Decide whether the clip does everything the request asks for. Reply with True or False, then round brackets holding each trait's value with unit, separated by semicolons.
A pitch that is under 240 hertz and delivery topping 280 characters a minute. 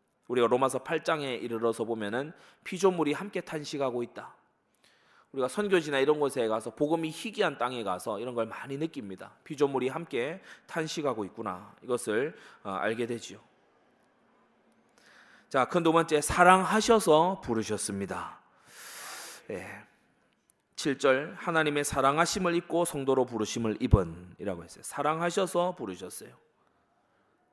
True (140 Hz; 290 characters per minute)